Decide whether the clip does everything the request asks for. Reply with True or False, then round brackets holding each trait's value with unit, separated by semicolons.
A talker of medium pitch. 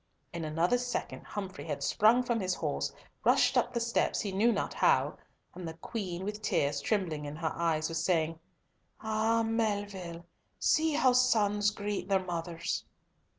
False (195 Hz)